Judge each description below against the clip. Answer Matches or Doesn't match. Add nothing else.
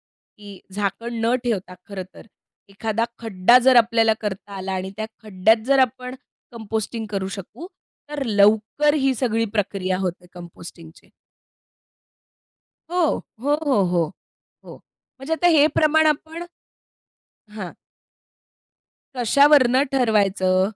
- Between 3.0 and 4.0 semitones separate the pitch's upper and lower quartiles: Doesn't match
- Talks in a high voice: Matches